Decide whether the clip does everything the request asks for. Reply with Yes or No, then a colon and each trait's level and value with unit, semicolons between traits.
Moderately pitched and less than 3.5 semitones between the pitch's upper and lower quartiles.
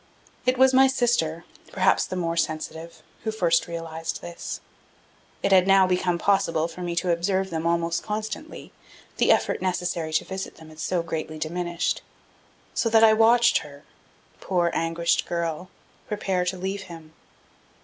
Yes: medium, 175 Hz; average, 2.8 semitones